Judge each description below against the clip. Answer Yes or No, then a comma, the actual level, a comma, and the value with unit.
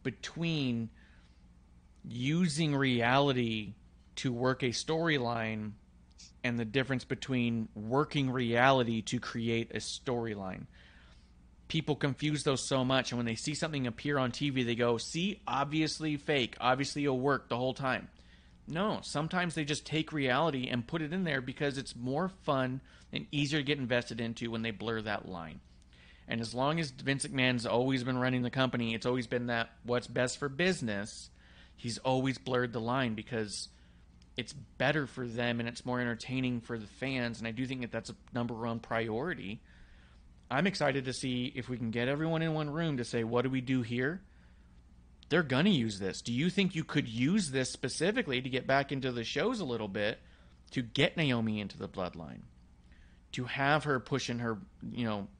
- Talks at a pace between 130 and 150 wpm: No, average, 180 wpm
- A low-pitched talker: Yes, low, 125 Hz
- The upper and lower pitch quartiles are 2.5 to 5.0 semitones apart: Yes, average, 3.9 semitones